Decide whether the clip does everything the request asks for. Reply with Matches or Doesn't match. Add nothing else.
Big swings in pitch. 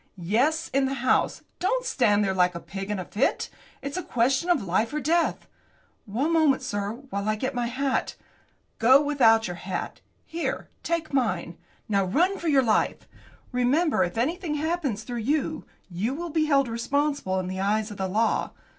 Matches